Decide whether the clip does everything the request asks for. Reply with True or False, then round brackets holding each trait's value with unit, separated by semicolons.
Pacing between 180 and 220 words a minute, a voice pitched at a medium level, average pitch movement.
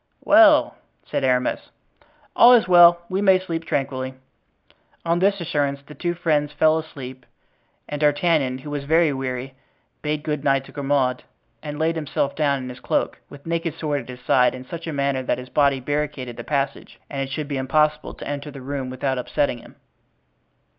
True (185 wpm; 145 Hz; 3.2 semitones)